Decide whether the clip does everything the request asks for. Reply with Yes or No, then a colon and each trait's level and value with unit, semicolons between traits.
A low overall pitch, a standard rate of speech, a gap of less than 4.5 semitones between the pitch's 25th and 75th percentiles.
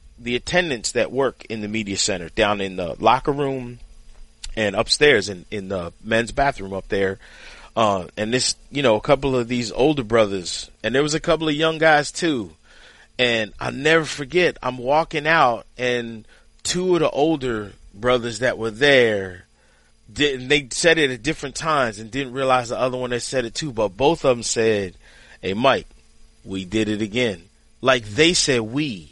No: low, 120 Hz; average, 185 wpm; average, 5.0 semitones